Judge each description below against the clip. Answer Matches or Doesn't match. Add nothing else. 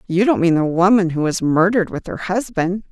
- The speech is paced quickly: Matches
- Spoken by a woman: Matches